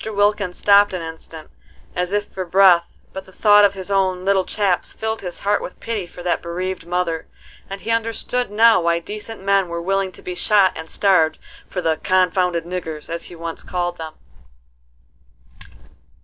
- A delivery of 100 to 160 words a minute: No, average, 175 wpm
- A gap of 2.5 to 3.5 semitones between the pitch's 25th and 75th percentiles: Yes, average, 2.8 semitones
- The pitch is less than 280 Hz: Yes, medium, 185 Hz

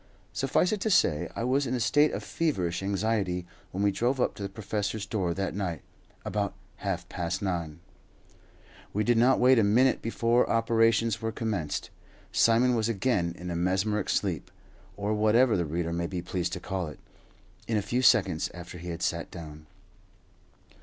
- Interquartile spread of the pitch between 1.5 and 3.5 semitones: No, average, 4.6 semitones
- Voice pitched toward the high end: No, low, 100 Hz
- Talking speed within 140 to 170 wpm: No, average, 180 wpm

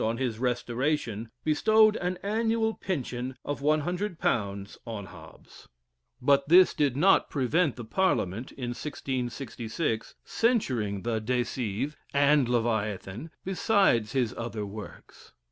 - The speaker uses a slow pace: Yes, slow, 115 wpm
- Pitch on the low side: Yes, low, 130 Hz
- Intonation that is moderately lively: No, wide, 5.9 semitones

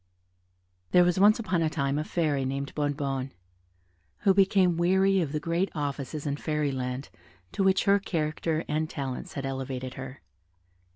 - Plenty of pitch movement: No, average, 4.4 semitones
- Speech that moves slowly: No, average, 160 wpm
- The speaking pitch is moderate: Yes, medium, 150 Hz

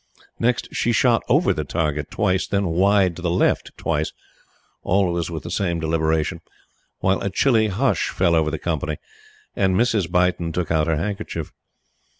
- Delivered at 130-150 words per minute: No, average, 160 wpm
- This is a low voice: Yes, very low, 90 Hz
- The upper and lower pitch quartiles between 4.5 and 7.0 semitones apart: No, average, 3.7 semitones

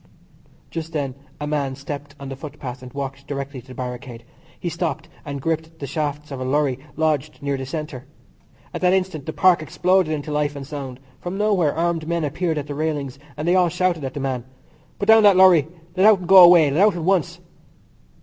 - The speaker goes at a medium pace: No, fast, 215 wpm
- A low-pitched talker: No, medium, 150 Hz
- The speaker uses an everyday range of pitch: Yes, average, 3.7 semitones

